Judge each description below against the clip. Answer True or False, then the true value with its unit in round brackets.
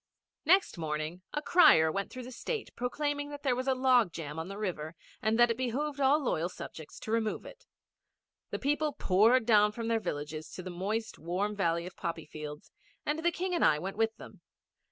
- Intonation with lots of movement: True (7.7 semitones)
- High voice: True (220 Hz)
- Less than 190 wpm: False (205 wpm)